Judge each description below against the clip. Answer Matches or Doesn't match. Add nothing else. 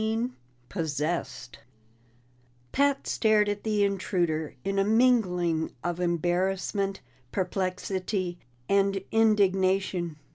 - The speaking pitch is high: Matches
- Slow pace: Matches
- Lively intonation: Doesn't match